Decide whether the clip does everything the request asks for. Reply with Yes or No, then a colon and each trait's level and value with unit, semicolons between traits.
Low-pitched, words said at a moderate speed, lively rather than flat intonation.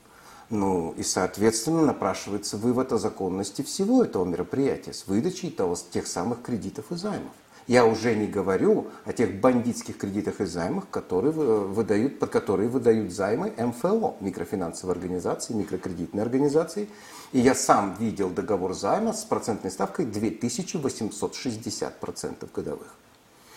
Yes: low, 110 Hz; average, 130 wpm; wide, 6.5 semitones